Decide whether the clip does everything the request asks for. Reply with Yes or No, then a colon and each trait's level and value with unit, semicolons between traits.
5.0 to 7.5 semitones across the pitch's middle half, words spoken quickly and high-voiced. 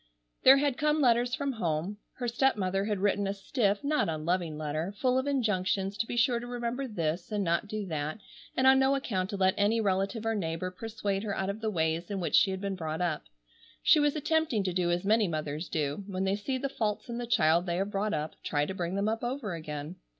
Yes: average, 5.3 semitones; fast, 235 wpm; high, 200 Hz